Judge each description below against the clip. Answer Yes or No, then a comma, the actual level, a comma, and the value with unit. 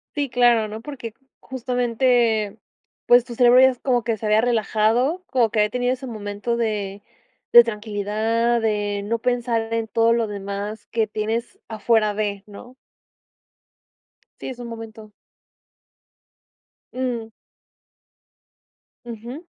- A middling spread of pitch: No, narrow, 2.3 semitones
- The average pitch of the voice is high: Yes, high, 230 Hz